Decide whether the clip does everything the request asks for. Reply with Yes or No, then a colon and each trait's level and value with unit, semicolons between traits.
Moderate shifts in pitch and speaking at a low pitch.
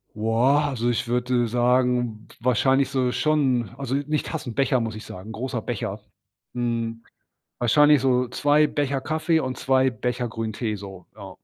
Yes: average, 3.0 semitones; low, 125 Hz